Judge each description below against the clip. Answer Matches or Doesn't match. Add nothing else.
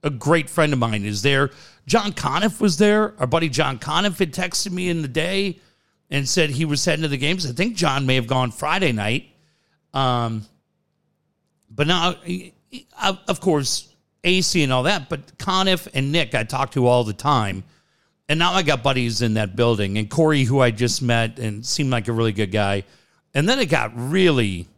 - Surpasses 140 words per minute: Matches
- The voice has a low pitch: Doesn't match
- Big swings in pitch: Matches